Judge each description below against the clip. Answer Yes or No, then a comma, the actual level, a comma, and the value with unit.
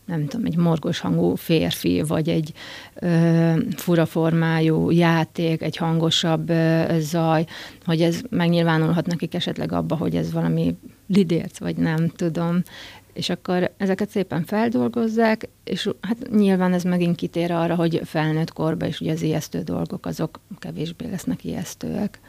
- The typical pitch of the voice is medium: Yes, medium, 165 Hz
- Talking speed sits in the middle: Yes, average, 145 wpm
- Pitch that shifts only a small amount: Yes, narrow, 1.9 semitones